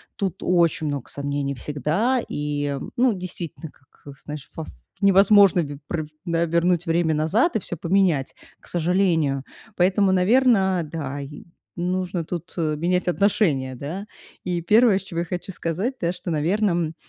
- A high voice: No, medium, 170 Hz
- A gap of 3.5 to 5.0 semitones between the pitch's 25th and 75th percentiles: Yes, average, 4.0 semitones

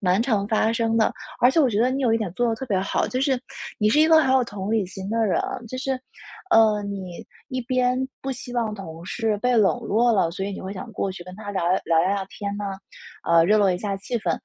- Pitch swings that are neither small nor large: Yes, average, 3.9 semitones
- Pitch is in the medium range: No, high, 215 Hz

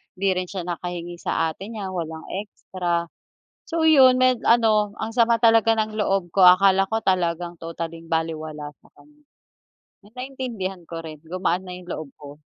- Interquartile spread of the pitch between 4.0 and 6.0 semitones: Yes, average, 4.8 semitones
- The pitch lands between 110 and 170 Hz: No, medium, 185 Hz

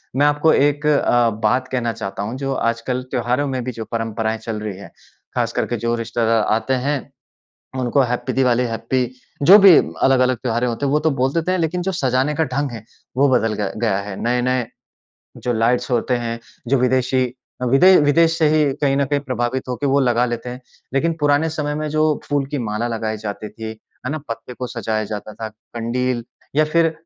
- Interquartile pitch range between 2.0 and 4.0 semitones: Yes, average, 3.7 semitones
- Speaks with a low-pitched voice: Yes, low, 125 Hz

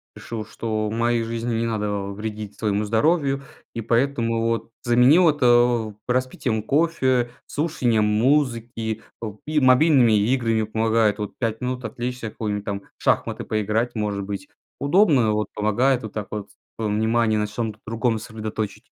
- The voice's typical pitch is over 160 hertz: No, low, 115 Hz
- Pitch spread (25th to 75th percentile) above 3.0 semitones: No, narrow, 2.6 semitones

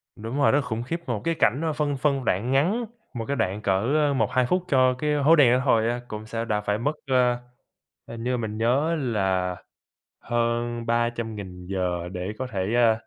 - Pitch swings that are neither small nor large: Yes, average, 4.2 semitones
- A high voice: No, low, 120 Hz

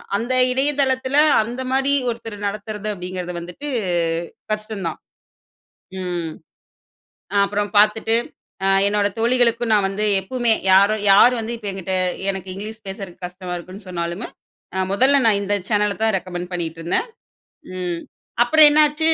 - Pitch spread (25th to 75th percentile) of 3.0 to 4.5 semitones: Yes, average, 4.2 semitones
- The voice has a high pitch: Yes, high, 205 Hz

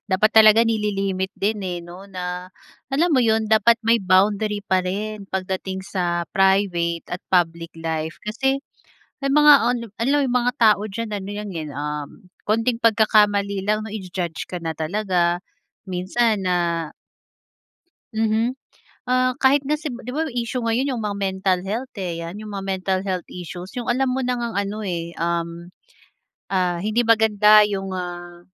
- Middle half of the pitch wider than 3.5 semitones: Yes, average, 4.0 semitones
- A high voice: Yes, high, 200 Hz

